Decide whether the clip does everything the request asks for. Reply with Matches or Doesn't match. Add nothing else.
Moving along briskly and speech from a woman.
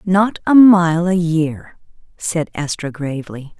Doesn't match